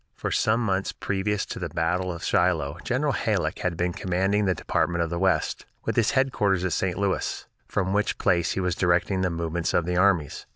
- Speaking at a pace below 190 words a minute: No, fast, 205 wpm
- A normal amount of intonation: No, narrow, 2.1 semitones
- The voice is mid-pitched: No, very low, 90 Hz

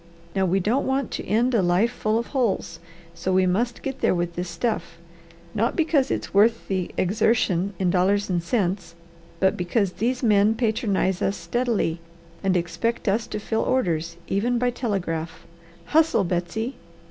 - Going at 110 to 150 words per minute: No, average, 165 wpm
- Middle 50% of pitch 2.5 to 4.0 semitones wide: No, average, 4.6 semitones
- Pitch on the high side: Yes, high, 200 Hz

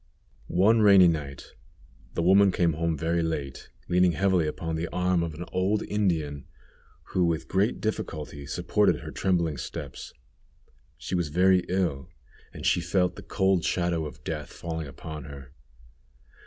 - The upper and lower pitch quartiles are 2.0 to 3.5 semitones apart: Yes, average, 2.9 semitones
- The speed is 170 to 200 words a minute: No, average, 150 wpm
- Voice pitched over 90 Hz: No, very low, 85 Hz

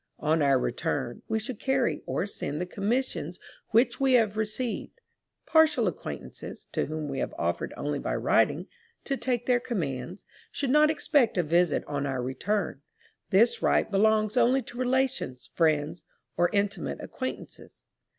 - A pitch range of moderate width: No, wide, 8.1 semitones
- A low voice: No, high, 210 Hz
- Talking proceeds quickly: No, average, 150 wpm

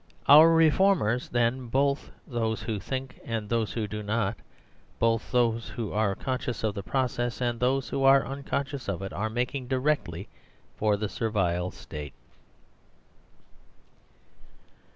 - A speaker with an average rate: No, slow, 120 wpm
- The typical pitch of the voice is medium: No, low, 115 Hz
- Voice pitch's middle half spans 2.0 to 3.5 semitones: No, average, 3.9 semitones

